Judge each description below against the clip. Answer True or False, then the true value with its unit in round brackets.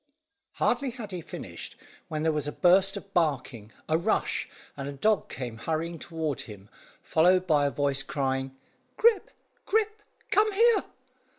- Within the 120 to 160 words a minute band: True (155 wpm)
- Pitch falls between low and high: True (160 Hz)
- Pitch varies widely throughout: True (6.2 semitones)